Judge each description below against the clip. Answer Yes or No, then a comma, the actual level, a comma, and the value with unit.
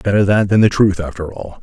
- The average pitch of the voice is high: No, very low, 95 Hz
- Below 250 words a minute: No, fast, 260 wpm